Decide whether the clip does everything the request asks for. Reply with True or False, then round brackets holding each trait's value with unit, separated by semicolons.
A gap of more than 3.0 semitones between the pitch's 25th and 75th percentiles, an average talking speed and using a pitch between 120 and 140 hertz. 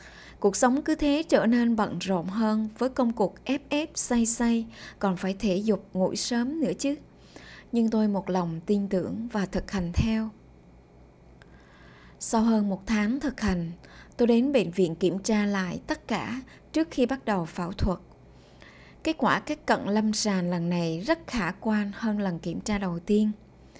False (4.4 semitones; 185 wpm; 210 Hz)